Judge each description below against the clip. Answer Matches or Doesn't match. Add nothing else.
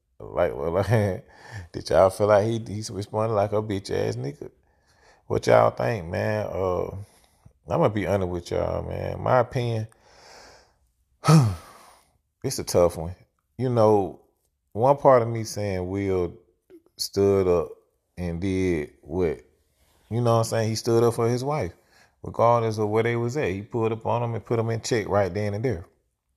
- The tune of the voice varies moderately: Matches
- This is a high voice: Doesn't match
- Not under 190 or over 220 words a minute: Doesn't match